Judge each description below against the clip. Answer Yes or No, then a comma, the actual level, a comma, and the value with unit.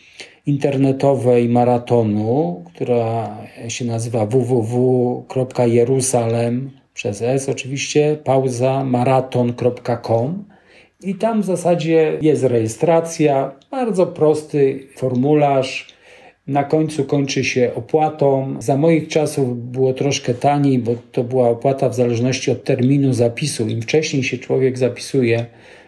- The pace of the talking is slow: Yes, slow, 105 wpm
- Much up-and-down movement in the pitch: No, average, 2.9 semitones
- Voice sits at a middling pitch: No, low, 130 Hz